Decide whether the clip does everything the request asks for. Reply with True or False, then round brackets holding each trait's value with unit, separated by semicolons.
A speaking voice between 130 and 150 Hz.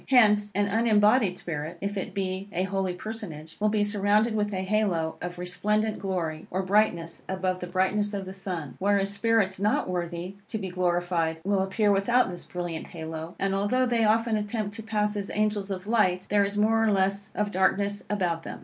False (195 Hz)